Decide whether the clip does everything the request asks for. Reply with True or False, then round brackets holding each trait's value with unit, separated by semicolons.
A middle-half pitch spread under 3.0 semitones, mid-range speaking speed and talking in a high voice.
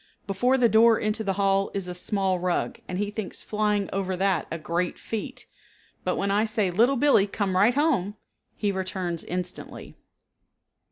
True (2.6 semitones; 170 wpm; 200 Hz)